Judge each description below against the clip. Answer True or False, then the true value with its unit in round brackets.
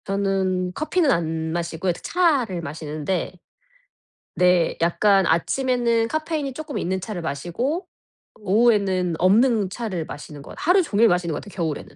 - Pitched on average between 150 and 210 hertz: True (190 Hz)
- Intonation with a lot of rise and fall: True (6.0 semitones)